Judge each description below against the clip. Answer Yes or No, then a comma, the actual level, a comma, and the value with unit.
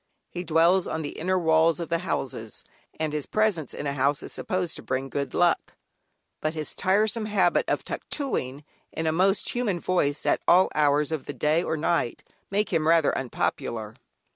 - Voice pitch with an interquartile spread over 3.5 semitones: Yes, average, 4.1 semitones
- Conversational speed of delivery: Yes, average, 180 wpm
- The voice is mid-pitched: Yes, medium, 160 Hz